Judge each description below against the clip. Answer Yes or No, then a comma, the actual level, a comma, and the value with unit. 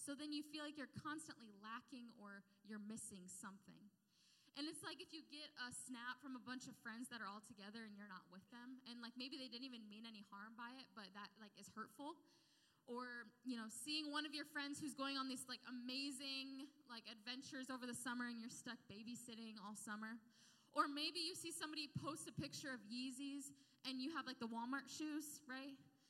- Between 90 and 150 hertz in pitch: No, very high, 250 Hz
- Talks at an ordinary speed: No, fast, 215 wpm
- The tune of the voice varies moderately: Yes, average, 4.0 semitones